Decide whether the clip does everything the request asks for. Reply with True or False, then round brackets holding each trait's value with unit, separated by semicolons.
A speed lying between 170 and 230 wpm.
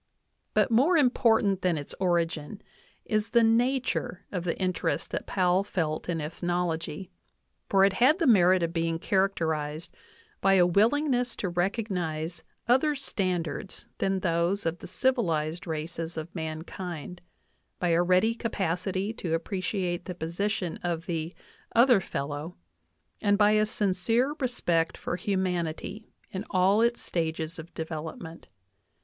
False (135 wpm)